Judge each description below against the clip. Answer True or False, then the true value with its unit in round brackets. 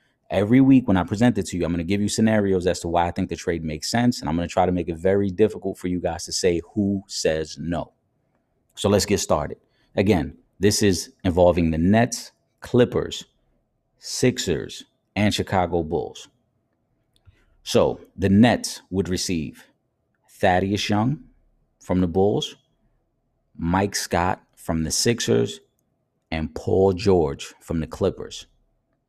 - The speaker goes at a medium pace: True (160 wpm)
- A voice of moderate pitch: False (95 Hz)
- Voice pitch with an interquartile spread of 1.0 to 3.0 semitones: False (4.0 semitones)